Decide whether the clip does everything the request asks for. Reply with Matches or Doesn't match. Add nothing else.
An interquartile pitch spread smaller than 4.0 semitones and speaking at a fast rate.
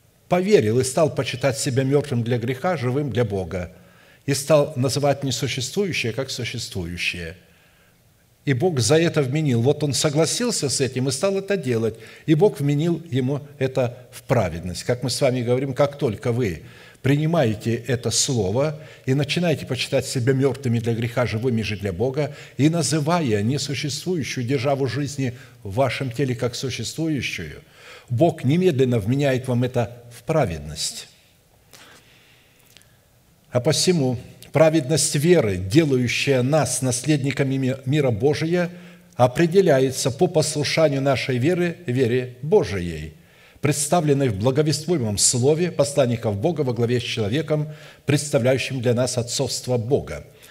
Doesn't match